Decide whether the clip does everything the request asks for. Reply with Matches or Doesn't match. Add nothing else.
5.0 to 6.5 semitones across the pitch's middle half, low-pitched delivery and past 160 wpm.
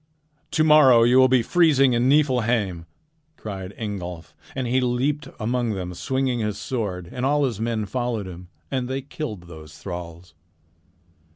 Doesn't match